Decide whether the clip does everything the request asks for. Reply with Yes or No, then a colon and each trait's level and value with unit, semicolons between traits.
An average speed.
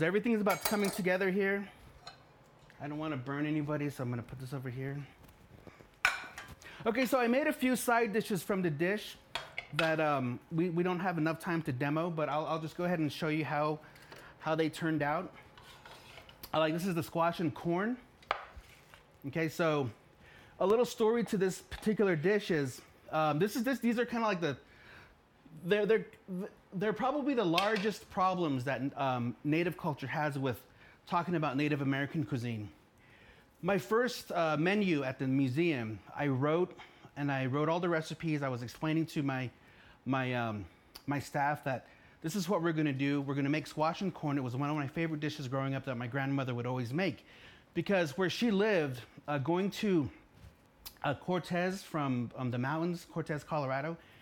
Yes: average, 190 wpm